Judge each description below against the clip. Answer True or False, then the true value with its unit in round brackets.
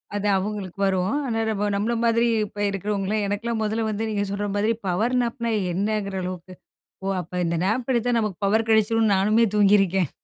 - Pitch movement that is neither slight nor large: False (2.3 semitones)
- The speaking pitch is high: True (210 Hz)